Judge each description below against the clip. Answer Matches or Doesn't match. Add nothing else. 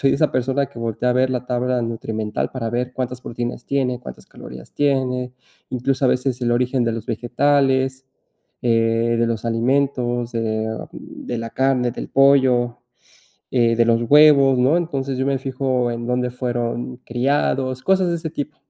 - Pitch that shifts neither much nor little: Doesn't match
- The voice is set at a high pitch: Doesn't match